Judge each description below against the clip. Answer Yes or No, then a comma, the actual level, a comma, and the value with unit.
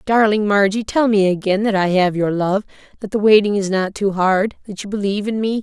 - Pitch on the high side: Yes, high, 200 Hz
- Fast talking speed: Yes, fast, 235 wpm